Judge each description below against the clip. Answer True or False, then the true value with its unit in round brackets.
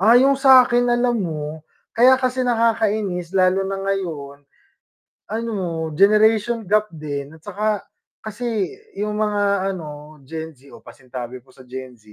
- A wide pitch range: True (6.6 semitones)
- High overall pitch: True (195 Hz)